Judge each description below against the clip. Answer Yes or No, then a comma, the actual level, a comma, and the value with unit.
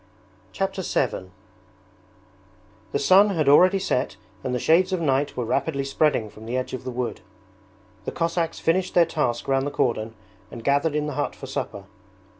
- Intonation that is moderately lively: Yes, average, 4.8 semitones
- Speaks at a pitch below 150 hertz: Yes, medium, 140 Hz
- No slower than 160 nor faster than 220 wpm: Yes, average, 175 wpm